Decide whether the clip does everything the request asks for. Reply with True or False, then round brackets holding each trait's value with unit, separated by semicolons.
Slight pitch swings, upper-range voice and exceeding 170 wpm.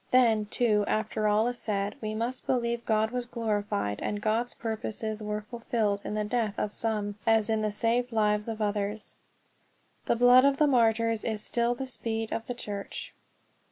True (2.0 semitones; 220 Hz; 180 wpm)